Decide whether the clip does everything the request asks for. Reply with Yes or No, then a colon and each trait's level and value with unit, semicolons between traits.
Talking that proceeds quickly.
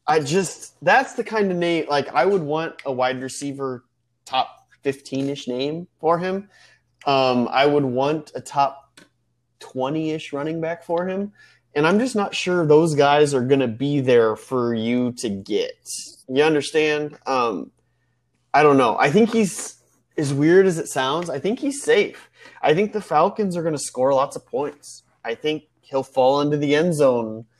No: average, 185 wpm